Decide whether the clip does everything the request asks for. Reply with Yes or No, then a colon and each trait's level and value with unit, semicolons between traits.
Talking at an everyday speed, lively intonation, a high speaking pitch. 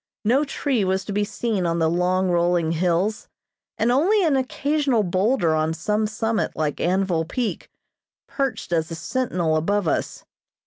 Yes: average, 160 wpm; wide, 6.0 semitones; high, 195 Hz